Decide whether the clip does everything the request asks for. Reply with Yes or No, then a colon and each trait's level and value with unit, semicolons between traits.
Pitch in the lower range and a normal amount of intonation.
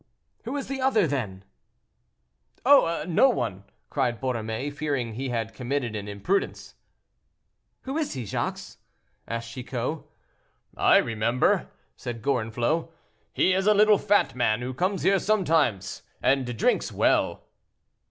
No: low, 130 Hz; wide, 8.4 semitones